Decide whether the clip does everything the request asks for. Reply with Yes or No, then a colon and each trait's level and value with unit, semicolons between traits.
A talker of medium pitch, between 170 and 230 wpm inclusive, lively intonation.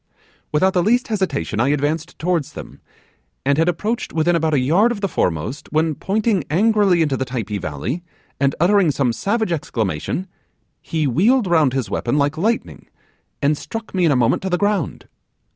Yes: medium, 160 Hz; average, 175 wpm; wide, 5.9 semitones